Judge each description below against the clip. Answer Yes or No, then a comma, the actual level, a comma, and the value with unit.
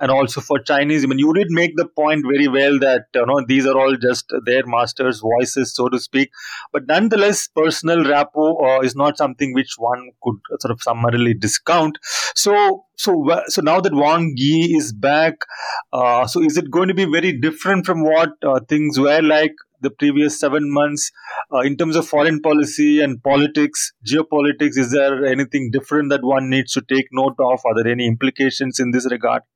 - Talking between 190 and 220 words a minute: Yes, average, 195 wpm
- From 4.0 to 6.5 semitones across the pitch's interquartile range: No, average, 2.8 semitones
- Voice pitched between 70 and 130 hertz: No, medium, 140 Hz